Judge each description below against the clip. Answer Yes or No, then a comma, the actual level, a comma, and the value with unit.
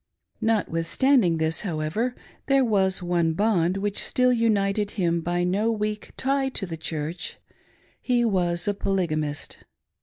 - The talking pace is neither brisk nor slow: No, slow, 130 wpm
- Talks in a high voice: Yes, high, 195 Hz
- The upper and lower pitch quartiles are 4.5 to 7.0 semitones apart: Yes, average, 4.8 semitones